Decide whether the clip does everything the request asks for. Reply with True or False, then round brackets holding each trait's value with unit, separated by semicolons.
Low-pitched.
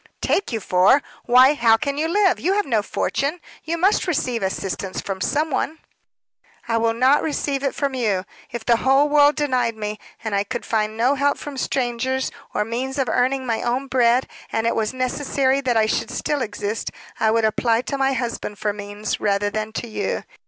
False (245 Hz)